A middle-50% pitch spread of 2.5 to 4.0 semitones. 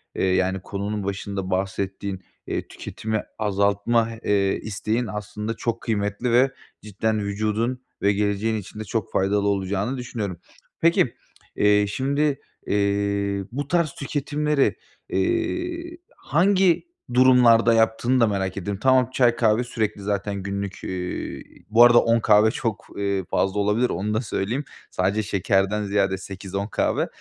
Yes: average, 3.3 semitones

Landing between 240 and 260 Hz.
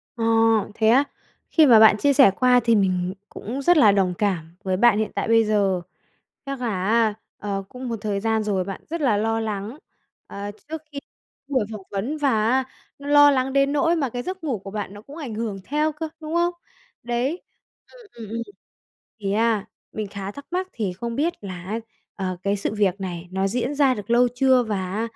No: high, 225 Hz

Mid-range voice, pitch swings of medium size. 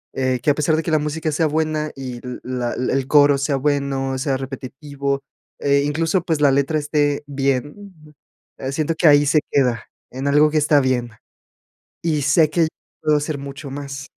No: medium, 145 Hz; narrow, 2.1 semitones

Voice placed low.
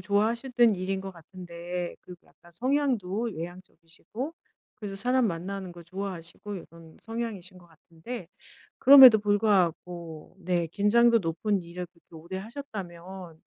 No: high, 190 Hz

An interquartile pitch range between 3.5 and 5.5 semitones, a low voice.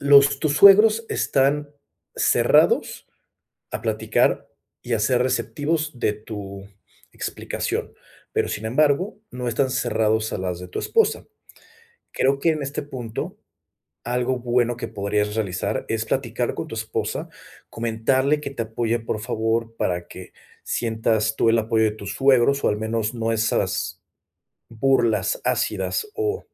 Yes: average, 4.0 semitones; low, 120 Hz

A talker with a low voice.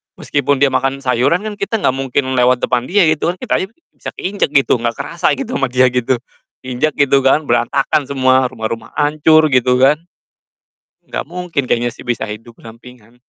Yes: low, 130 Hz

